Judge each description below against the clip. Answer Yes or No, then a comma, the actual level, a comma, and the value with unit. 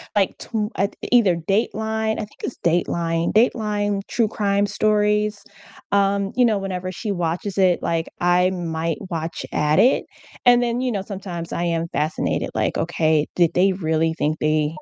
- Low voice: No, high, 190 Hz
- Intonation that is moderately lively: Yes, average, 4.0 semitones